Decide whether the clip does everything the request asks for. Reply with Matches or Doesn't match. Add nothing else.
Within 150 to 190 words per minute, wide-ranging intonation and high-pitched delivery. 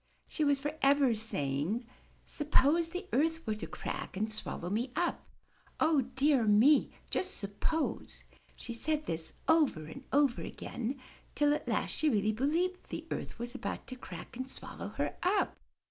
Matches